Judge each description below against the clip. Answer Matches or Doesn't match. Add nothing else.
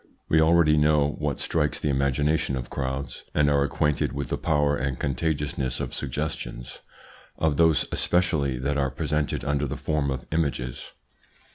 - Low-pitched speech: Matches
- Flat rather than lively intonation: Matches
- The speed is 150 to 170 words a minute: Matches